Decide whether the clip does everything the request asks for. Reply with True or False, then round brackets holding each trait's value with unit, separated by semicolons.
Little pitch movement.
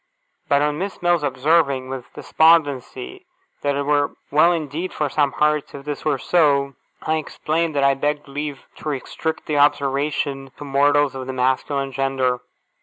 True (1.9 semitones)